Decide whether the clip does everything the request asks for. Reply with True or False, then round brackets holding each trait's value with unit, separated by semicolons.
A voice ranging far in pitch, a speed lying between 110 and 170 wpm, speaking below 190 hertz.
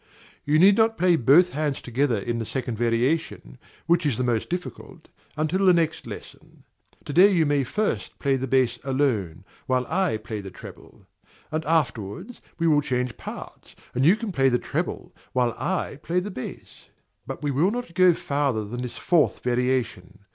False (5.8 semitones; 180 wpm; 140 Hz)